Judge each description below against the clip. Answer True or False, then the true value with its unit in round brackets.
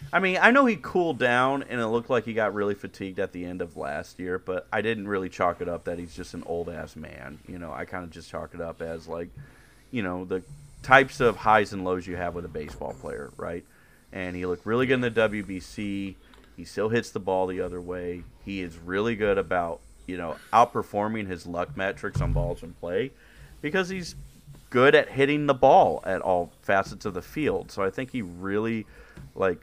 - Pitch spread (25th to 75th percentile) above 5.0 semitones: True (5.6 semitones)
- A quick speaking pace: True (225 wpm)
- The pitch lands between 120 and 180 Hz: False (95 Hz)